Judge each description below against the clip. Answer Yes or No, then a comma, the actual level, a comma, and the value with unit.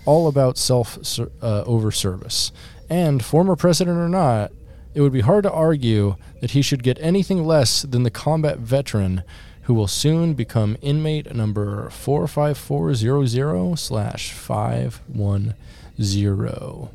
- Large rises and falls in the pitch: Yes, wide, 5.9 semitones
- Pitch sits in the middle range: No, low, 130 Hz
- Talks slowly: Yes, slow, 125 wpm